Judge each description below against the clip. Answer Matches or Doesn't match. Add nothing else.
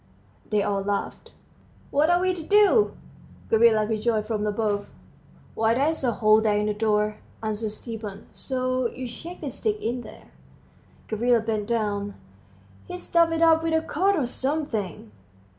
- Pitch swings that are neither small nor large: Doesn't match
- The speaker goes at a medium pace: Matches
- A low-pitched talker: Doesn't match